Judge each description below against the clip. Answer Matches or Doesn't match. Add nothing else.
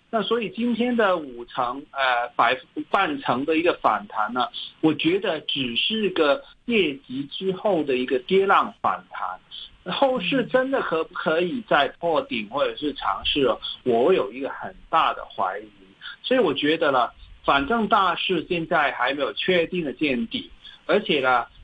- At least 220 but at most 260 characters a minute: Matches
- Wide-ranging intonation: Matches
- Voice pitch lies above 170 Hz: Matches